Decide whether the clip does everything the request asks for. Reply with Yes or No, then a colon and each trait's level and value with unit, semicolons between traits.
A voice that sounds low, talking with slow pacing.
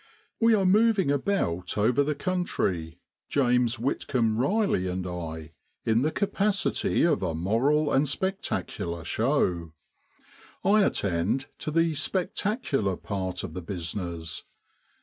Yes: low, 125 Hz; slow, 120 wpm